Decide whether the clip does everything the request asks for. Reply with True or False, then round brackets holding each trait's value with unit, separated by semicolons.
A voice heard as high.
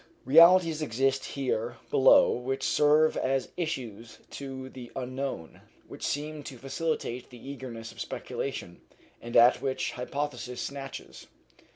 False (135 Hz)